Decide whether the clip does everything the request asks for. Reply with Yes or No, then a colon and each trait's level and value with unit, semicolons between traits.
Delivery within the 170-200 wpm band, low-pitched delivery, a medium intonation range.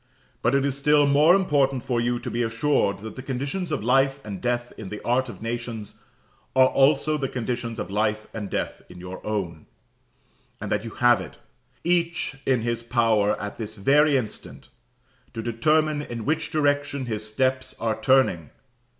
Yes: average, 175 wpm; low, 125 Hz; average, 4.2 semitones